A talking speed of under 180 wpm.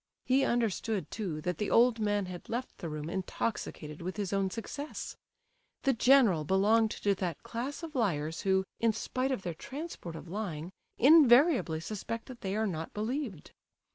Yes: average, 170 wpm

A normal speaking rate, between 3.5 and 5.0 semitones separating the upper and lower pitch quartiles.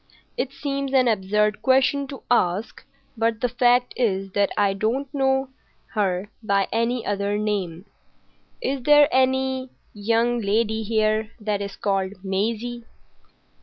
No: slow, 130 wpm; average, 4.1 semitones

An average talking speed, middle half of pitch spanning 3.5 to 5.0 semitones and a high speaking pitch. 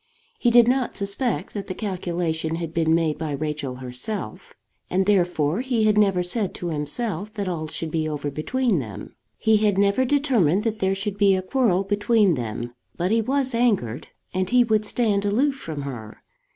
No: average, 185 wpm; wide, 5.6 semitones; high, 195 Hz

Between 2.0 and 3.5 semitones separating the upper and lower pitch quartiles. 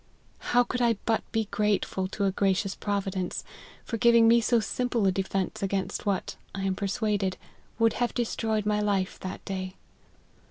Yes: average, 2.8 semitones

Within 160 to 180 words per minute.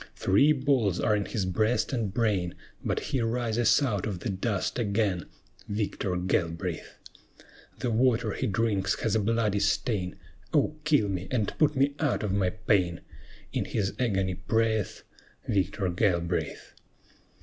No: average, 145 wpm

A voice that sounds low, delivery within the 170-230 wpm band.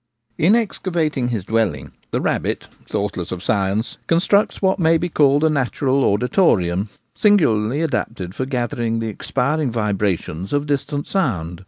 No: low, 125 Hz; average, 145 wpm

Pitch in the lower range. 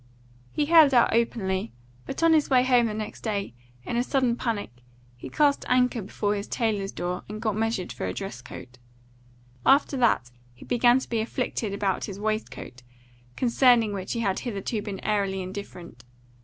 No: high, 215 Hz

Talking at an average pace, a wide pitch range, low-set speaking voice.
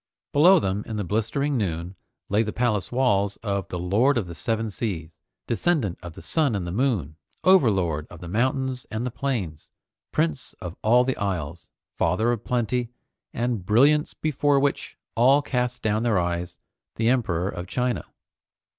Yes: average, 165 wpm; wide, 5.8 semitones; low, 110 Hz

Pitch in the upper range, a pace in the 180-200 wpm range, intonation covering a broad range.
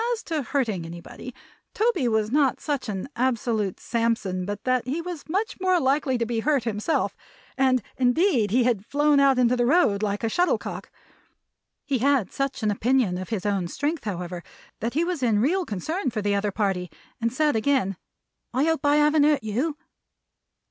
Yes: very high, 250 Hz; average, 185 wpm; wide, 5.7 semitones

